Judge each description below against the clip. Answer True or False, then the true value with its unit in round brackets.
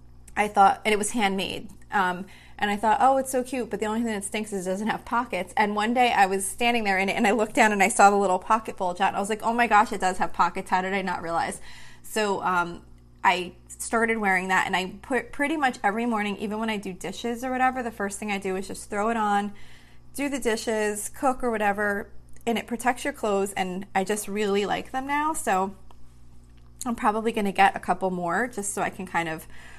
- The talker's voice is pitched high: True (205 Hz)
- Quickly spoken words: True (250 wpm)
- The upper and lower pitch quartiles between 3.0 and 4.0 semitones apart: True (3.4 semitones)